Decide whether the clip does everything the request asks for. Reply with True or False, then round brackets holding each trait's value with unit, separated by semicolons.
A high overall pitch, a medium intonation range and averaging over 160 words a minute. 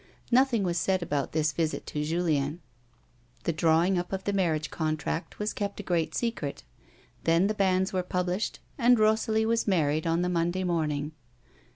False (175 Hz; 3.8 semitones; 170 wpm)